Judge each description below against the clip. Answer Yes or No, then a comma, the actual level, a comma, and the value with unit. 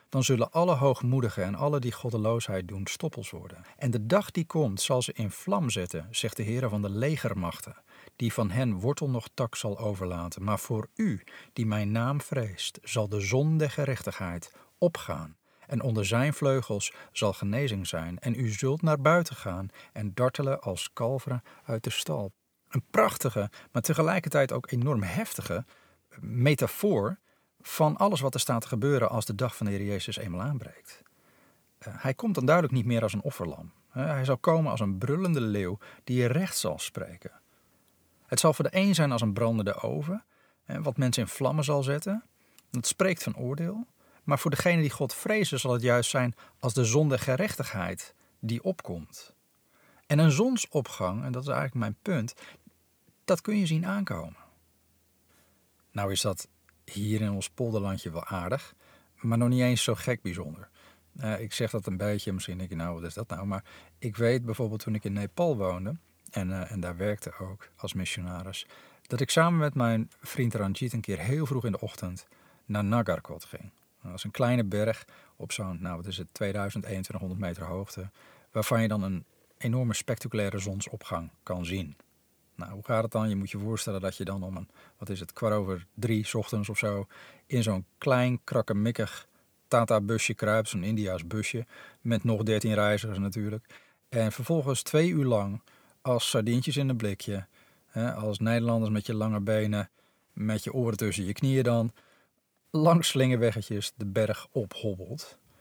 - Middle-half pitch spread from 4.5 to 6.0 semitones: Yes, average, 4.9 semitones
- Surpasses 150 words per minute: Yes, average, 180 wpm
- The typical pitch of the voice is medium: No, low, 115 Hz